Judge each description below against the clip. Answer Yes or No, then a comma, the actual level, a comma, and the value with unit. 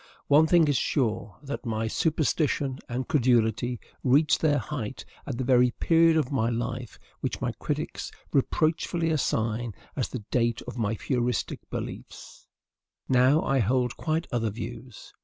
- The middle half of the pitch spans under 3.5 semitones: No, average, 4.0 semitones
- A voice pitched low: Yes, low, 125 Hz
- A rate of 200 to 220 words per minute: No, average, 145 wpm